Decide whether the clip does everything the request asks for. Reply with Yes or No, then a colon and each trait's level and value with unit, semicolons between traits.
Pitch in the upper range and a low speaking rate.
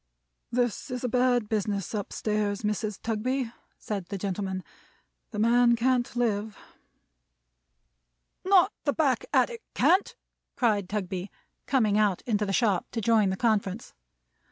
Yes: high, 215 Hz; slow, 130 wpm